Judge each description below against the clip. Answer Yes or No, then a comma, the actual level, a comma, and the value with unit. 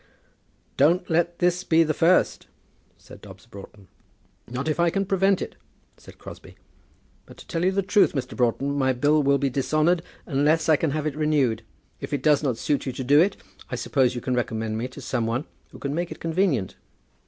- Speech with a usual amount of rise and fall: Yes, average, 4.6 semitones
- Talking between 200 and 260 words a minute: Yes, fast, 205 wpm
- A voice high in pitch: No, medium, 145 Hz